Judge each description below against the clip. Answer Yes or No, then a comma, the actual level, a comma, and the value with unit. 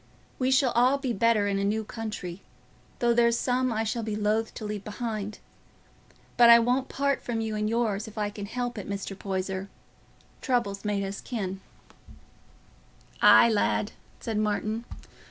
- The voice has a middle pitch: No, high, 220 Hz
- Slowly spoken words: No, average, 165 wpm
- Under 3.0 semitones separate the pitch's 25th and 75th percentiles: Yes, narrow, 2.6 semitones